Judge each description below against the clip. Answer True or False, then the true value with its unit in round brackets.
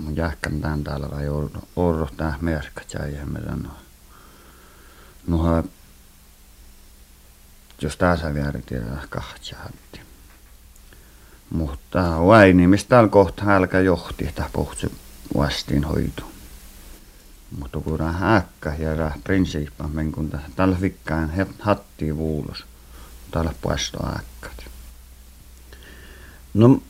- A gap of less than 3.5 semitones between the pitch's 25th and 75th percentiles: False (4.4 semitones)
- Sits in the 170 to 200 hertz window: False (75 Hz)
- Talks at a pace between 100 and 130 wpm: True (110 wpm)